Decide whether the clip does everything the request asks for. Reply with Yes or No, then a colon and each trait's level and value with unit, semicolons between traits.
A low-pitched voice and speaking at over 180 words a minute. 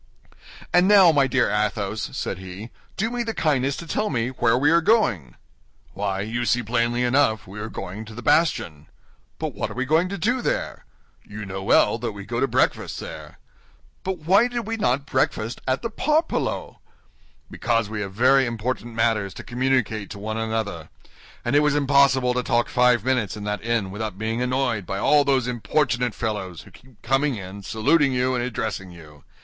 Yes: low, 120 Hz; average, 190 wpm